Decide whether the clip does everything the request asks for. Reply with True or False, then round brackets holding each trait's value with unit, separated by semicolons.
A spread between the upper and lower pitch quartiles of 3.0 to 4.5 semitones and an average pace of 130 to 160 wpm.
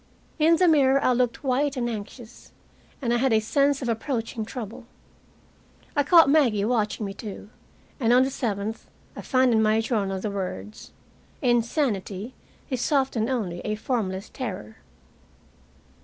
True (3.8 semitones; 150 wpm)